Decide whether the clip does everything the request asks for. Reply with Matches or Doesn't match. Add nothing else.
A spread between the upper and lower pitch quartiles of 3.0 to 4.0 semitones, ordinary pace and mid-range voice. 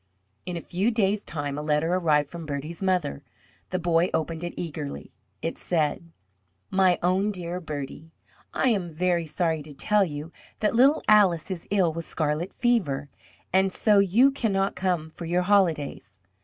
Matches